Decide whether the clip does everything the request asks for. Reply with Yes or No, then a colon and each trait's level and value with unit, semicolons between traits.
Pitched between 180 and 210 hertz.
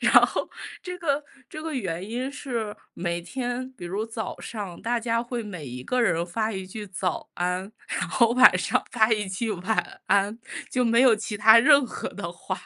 No: high, 220 Hz